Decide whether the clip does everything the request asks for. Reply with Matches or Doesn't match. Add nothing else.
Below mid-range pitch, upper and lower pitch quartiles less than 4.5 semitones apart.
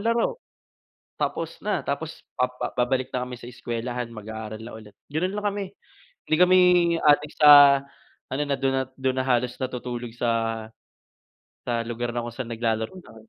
Matches